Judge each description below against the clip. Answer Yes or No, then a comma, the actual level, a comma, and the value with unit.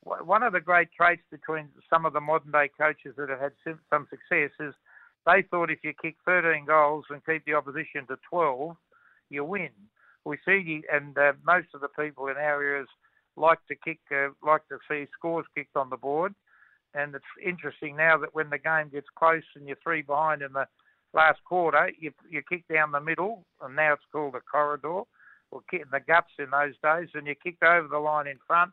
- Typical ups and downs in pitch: No, narrow, 2.2 semitones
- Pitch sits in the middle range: Yes, medium, 150 Hz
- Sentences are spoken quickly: Yes, fast, 210 wpm